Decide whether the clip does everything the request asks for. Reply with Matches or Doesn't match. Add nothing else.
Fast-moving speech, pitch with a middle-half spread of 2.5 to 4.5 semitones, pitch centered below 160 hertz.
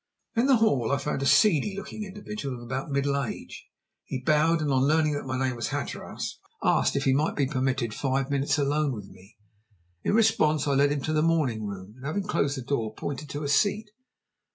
Matches